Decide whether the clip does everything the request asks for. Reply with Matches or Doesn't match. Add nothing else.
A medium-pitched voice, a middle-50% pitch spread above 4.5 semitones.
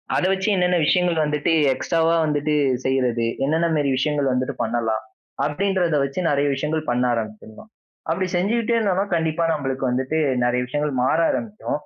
Matches